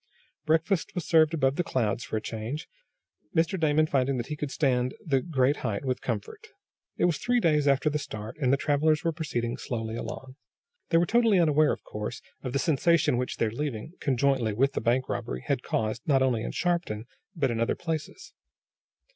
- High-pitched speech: No, medium, 140 Hz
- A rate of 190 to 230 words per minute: Yes, average, 195 wpm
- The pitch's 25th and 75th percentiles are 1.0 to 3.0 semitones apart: No, average, 4.7 semitones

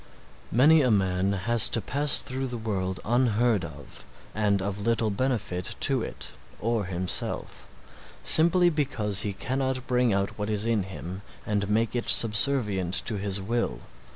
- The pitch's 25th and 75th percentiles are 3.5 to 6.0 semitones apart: Yes, average, 3.9 semitones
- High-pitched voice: No, low, 105 Hz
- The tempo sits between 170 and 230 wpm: No, average, 155 wpm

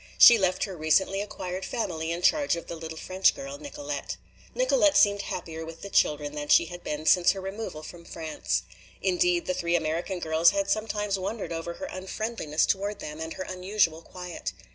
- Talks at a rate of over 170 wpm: Yes, average, 185 wpm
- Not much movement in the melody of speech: No, average, 4.3 semitones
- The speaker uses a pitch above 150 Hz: Yes, medium, 185 Hz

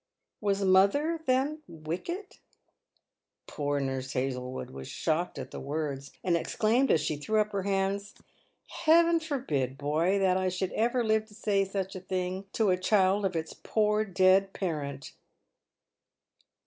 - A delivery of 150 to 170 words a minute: Yes, average, 160 wpm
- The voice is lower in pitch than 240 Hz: Yes, high, 190 Hz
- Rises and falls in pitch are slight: No, wide, 5.6 semitones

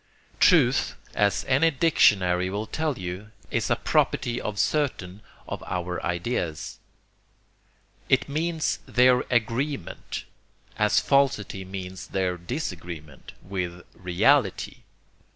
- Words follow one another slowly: Yes, slow, 100 wpm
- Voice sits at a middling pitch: No, low, 100 Hz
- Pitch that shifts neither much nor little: No, wide, 6.2 semitones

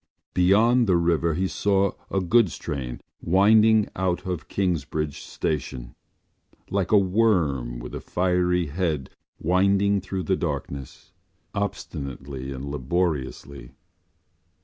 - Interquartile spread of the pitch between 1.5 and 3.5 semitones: No, wide, 5.5 semitones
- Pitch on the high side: No, very low, 90 Hz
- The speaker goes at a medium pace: No, slow, 110 wpm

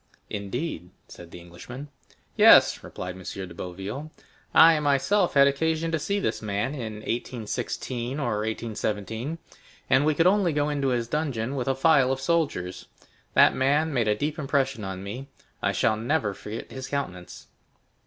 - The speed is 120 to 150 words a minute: No, average, 160 wpm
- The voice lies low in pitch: Yes, low, 130 Hz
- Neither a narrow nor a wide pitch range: No, wide, 5.8 semitones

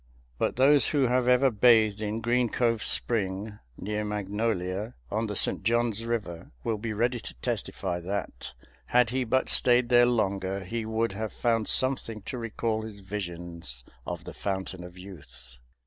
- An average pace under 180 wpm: Yes, average, 165 wpm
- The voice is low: Yes, low, 110 Hz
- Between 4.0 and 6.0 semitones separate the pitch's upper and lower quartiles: No, average, 3.6 semitones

